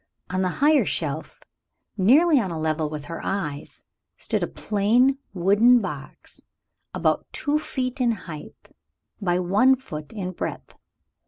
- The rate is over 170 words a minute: No, average, 140 wpm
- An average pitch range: No, wide, 6.9 semitones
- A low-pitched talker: No, high, 195 Hz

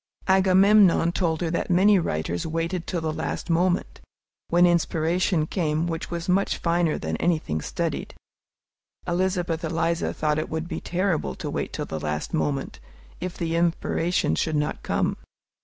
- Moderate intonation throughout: No, narrow, 2.2 semitones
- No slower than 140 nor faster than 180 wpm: Yes, average, 155 wpm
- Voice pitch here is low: No, medium, 170 Hz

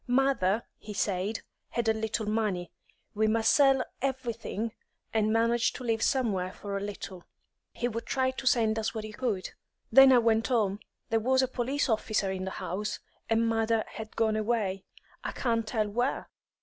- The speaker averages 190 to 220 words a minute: No, average, 175 wpm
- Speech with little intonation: Yes, narrow, 2.3 semitones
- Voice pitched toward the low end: No, high, 225 Hz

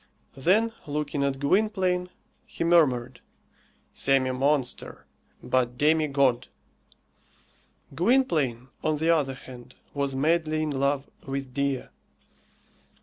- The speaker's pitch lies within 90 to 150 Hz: Yes, medium, 140 Hz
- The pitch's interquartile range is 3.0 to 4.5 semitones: Yes, average, 3.4 semitones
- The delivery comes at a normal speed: No, slow, 100 wpm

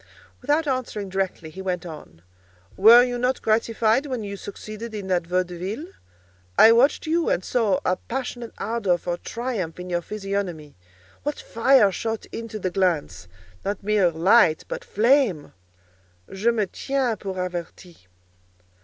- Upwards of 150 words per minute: No, average, 145 wpm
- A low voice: No, high, 205 Hz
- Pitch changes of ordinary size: Yes, average, 4.6 semitones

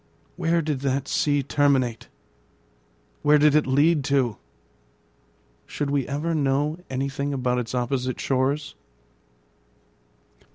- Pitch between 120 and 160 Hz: Yes, medium, 140 Hz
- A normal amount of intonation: No, narrow, 2.1 semitones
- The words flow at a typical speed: No, slow, 110 wpm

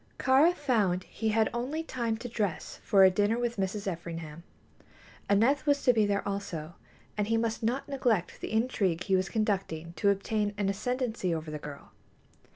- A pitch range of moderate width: Yes, average, 4.2 semitones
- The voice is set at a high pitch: Yes, high, 210 Hz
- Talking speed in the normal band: Yes, average, 175 wpm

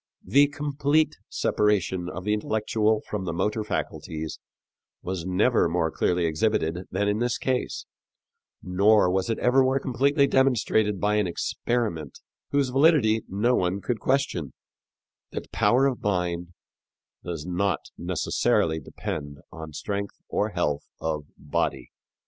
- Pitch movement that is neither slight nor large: No, wide, 5.9 semitones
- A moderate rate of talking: No, slow, 130 wpm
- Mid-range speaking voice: No, low, 105 Hz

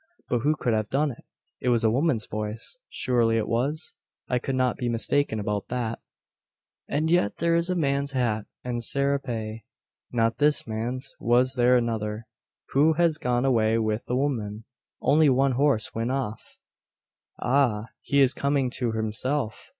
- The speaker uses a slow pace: No, average, 165 wpm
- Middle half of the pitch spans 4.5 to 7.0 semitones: No, average, 3.8 semitones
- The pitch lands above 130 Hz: No, low, 125 Hz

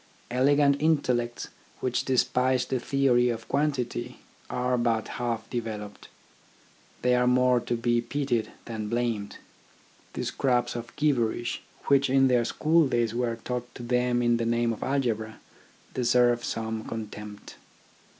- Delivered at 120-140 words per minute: Yes, slow, 135 wpm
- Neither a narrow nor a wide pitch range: No, narrow, 1.7 semitones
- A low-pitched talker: Yes, low, 120 Hz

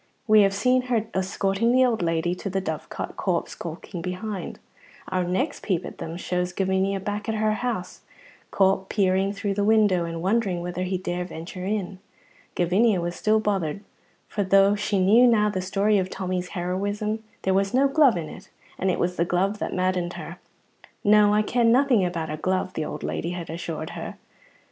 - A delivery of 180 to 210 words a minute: Yes, average, 190 wpm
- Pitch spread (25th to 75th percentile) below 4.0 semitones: Yes, average, 2.9 semitones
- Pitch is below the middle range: No, high, 190 Hz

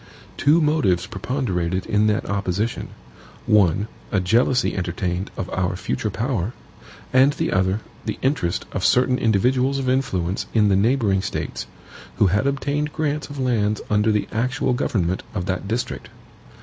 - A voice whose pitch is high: No, low, 105 Hz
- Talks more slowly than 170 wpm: Yes, average, 150 wpm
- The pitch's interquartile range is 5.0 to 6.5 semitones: Yes, wide, 5.5 semitones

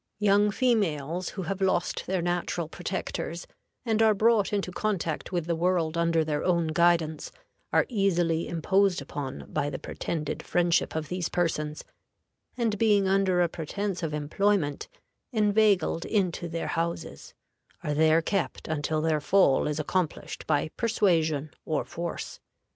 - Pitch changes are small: No, average, 3.7 semitones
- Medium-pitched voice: Yes, medium, 170 Hz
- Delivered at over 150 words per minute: No, average, 140 wpm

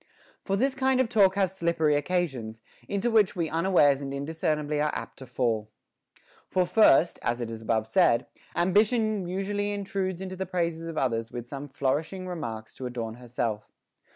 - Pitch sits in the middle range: Yes, medium, 165 Hz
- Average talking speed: Yes, average, 170 wpm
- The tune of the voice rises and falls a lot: Yes, wide, 7.4 semitones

